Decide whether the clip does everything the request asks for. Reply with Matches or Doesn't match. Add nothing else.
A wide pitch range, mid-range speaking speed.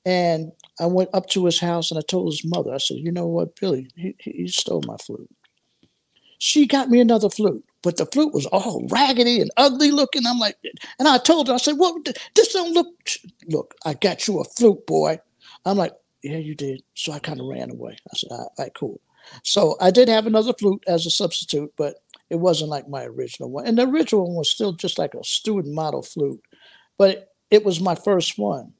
Doesn't match